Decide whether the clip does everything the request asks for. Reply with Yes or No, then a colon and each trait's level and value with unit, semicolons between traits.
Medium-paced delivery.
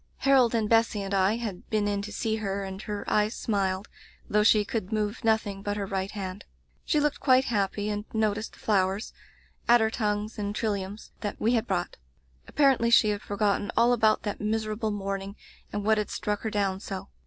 No: fast, 210 wpm